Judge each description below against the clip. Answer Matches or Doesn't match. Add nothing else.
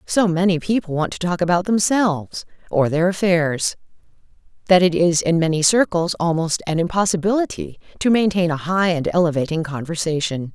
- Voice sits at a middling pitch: Matches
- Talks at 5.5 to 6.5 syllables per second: Doesn't match